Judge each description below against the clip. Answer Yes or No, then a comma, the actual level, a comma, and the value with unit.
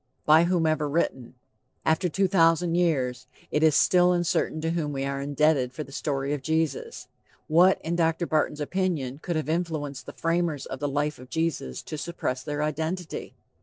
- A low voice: No, medium, 155 Hz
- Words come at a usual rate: Yes, average, 175 wpm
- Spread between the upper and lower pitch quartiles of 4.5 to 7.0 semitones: No, average, 3.0 semitones